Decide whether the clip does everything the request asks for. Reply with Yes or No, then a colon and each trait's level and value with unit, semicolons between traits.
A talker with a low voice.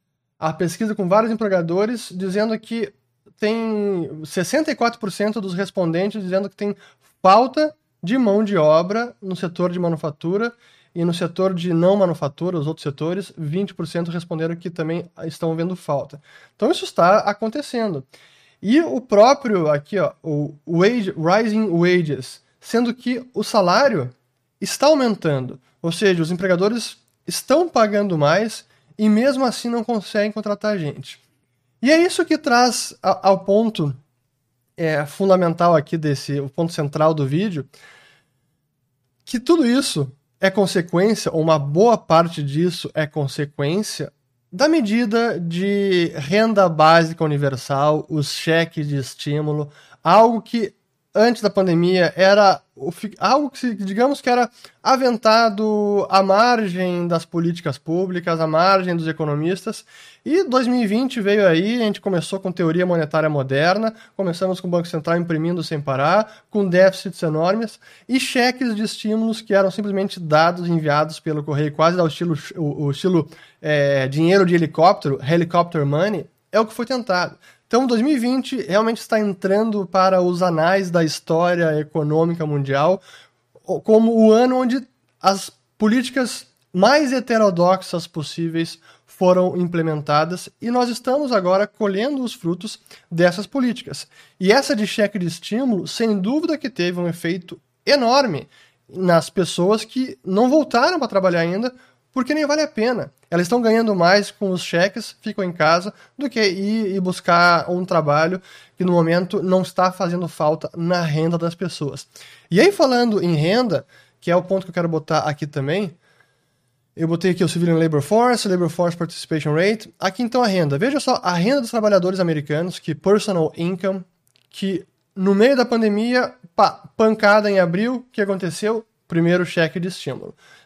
No: medium, 185 Hz